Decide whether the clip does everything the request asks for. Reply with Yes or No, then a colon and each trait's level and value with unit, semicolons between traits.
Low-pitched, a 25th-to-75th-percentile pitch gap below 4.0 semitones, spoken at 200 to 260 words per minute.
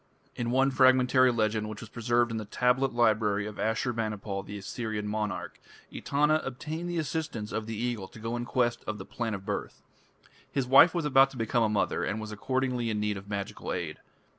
Yes: low, 115 Hz; average, 3.4 semitones; fast, 205 wpm